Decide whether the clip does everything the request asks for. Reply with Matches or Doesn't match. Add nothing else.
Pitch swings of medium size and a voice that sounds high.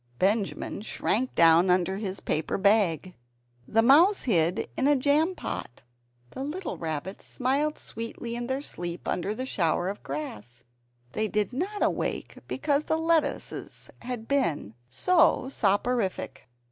Doesn't match